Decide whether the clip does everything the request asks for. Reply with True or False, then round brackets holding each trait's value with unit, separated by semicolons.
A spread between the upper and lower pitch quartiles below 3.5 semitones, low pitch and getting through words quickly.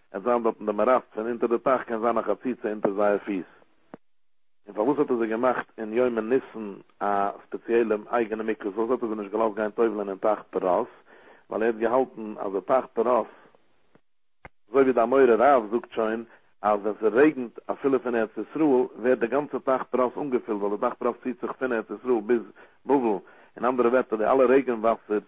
True (2.7 semitones; 115 Hz; 215 wpm)